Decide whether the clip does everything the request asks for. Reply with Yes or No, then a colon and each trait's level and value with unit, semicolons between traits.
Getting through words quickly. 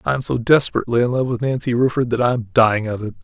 Yes: fast, 280 wpm